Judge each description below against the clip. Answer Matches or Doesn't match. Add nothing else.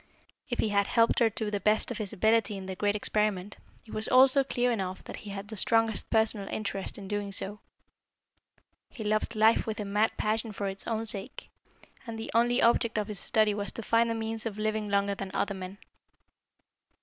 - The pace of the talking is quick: Matches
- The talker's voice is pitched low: Doesn't match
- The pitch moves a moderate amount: Doesn't match